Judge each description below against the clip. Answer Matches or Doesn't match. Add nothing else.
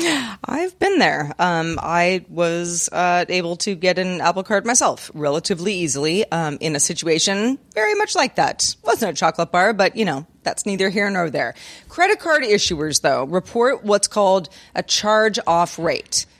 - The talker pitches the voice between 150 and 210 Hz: Matches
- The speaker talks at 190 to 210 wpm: Doesn't match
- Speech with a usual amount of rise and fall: Matches